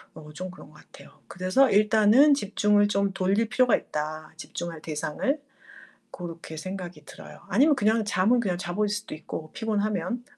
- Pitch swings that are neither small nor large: Yes, average, 4.1 semitones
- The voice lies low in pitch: No, high, 200 Hz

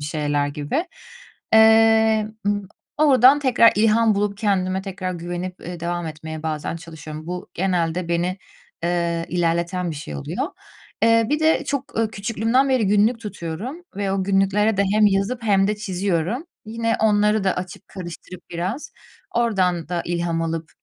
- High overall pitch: Yes, high, 195 Hz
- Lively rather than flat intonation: No, average, 4.5 semitones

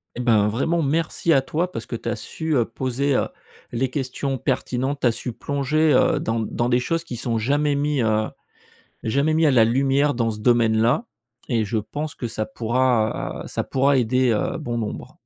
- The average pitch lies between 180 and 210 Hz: No, low, 130 Hz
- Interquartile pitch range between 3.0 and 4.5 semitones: Yes, average, 3.7 semitones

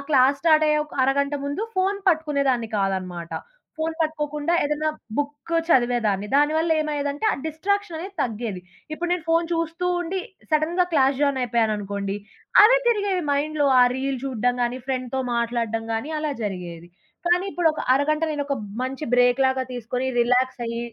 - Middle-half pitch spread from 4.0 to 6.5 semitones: Yes, average, 4.8 semitones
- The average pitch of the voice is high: Yes, very high, 280 Hz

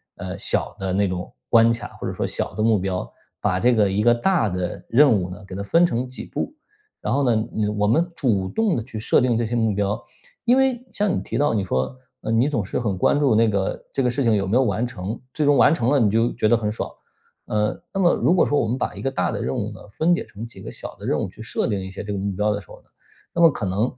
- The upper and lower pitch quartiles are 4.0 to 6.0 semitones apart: Yes, average, 4.7 semitones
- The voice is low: Yes, low, 115 Hz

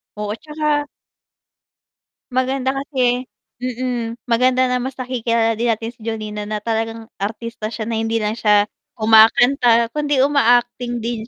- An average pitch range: No, narrow, 2.3 semitones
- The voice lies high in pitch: Yes, high, 235 Hz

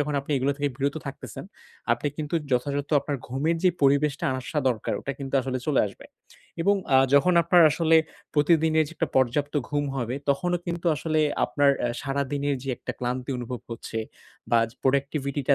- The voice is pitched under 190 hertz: Yes, medium, 140 Hz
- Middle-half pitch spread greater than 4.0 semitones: No, narrow, 2.4 semitones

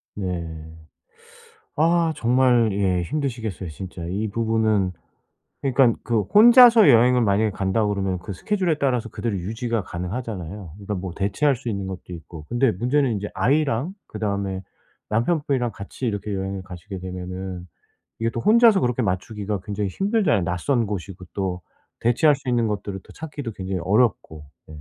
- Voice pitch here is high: No, low, 105 Hz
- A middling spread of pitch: Yes, average, 4.9 semitones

